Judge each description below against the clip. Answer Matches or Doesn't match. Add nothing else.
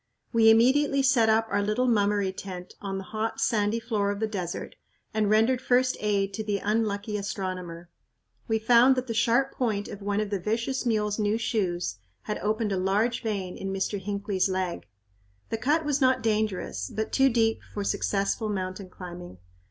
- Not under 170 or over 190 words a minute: Matches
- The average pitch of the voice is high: Matches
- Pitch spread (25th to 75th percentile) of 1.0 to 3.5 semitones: Matches